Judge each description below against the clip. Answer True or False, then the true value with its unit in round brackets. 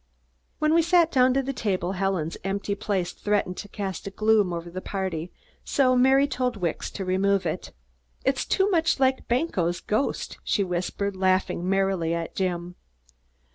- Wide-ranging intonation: True (5.7 semitones)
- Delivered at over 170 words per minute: False (165 wpm)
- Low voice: False (200 Hz)